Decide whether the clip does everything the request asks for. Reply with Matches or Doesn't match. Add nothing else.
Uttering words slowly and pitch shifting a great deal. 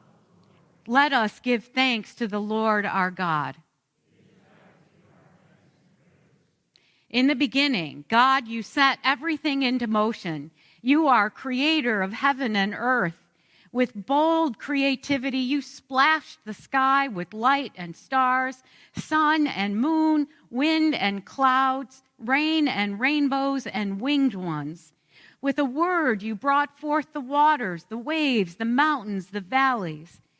Matches